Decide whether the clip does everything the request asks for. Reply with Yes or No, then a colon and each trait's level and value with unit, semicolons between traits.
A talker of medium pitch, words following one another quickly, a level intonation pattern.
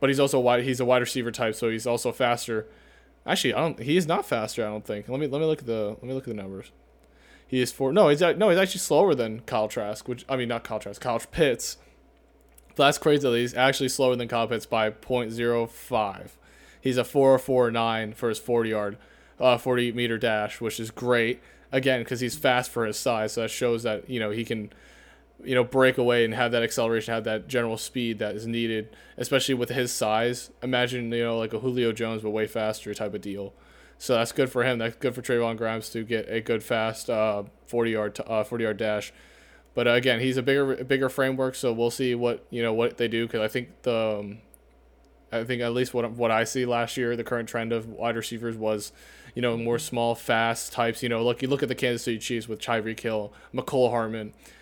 No: low, 115 Hz; fast, 230 wpm; narrow, 2.2 semitones